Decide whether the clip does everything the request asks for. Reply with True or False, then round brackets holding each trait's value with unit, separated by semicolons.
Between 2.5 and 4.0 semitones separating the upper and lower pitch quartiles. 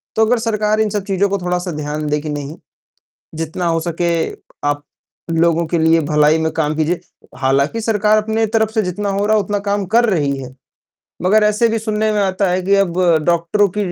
False (4.7 semitones)